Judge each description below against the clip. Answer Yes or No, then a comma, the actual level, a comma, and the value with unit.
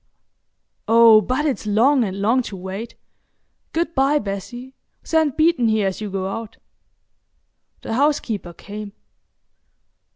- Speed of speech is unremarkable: No, slow, 120 wpm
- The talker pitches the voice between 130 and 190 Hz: No, high, 225 Hz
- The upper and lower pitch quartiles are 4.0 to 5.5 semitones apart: Yes, average, 4.9 semitones